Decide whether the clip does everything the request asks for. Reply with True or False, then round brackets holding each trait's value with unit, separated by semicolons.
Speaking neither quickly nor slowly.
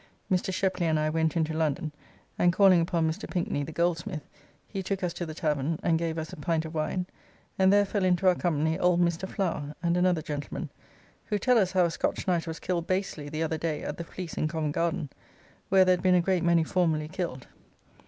False (220 wpm)